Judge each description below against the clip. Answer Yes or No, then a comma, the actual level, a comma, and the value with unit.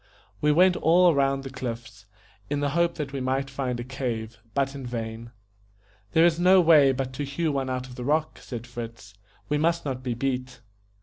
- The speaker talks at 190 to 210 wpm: Yes, average, 200 wpm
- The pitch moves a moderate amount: Yes, average, 3.2 semitones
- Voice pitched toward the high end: No, low, 135 Hz